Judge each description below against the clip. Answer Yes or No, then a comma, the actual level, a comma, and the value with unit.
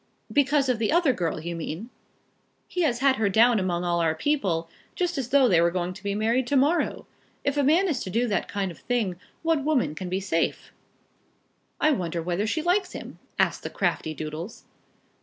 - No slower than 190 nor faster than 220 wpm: Yes, fast, 205 wpm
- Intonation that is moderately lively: No, wide, 8.2 semitones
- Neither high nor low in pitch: No, high, 225 Hz